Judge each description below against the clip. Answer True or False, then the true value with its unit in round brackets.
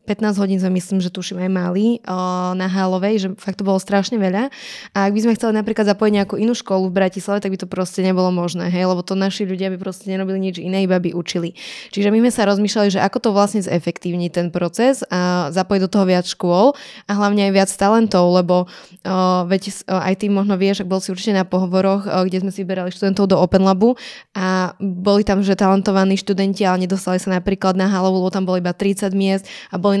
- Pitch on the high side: True (195 Hz)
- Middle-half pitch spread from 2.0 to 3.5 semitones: False (1.5 semitones)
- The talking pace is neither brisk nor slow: False (225 wpm)